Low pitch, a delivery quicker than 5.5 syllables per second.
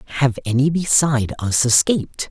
Yes: low, 130 Hz; 5.7 syllables/s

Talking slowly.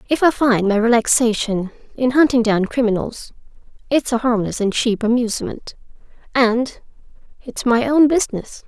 Yes: slow, 130 wpm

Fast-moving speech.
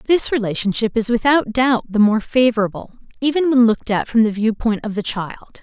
No: average, 190 wpm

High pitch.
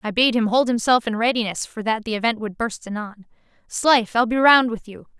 Yes: high, 230 Hz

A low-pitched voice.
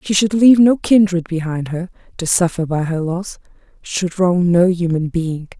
No: medium, 175 Hz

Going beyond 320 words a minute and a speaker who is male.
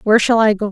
No: fast, 335 wpm; female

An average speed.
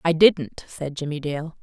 Yes: average, 185 wpm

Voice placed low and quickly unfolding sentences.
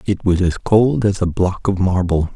Yes: very low, 95 Hz; fast, 230 wpm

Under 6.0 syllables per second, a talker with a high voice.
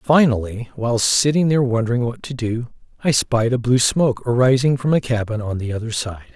No: 5.7 syllables/s; low, 120 Hz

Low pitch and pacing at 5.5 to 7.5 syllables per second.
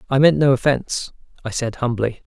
Yes: low, 130 Hz; 5.8 syllables/s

